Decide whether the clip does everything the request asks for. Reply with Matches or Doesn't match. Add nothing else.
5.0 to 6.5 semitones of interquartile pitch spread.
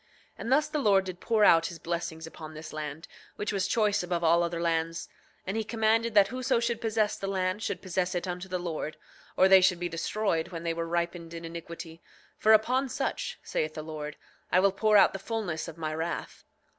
Doesn't match